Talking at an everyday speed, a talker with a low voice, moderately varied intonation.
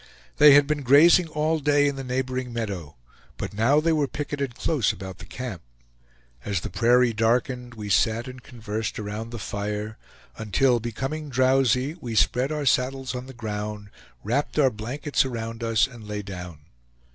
Yes: average, 170 wpm; low, 125 Hz; average, 4.1 semitones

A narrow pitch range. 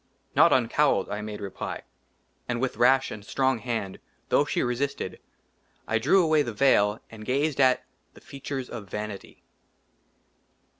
No: average, 4.2 semitones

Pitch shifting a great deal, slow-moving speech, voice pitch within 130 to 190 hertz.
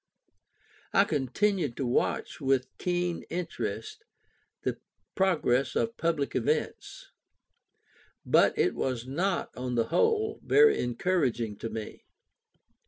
Yes: wide, 7.1 semitones; slow, 105 wpm; medium, 140 Hz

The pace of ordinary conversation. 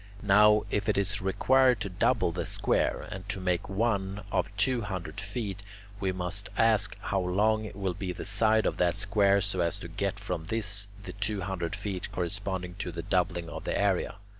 Yes: average, 190 wpm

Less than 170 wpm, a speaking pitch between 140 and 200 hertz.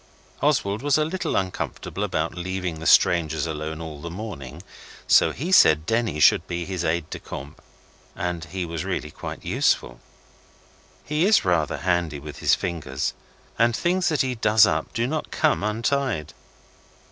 No: average, 160 wpm; very low, 90 Hz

